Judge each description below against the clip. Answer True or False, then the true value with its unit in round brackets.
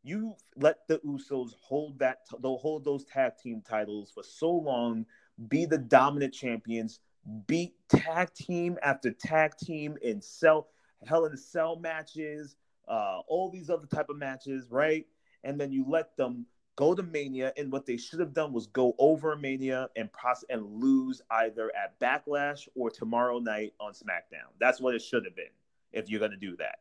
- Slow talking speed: False (185 wpm)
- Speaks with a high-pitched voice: False (140 Hz)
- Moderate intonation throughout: True (4.8 semitones)